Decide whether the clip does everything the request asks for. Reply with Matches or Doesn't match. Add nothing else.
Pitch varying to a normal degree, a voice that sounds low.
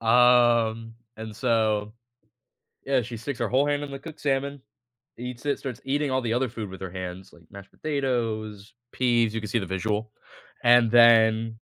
Matches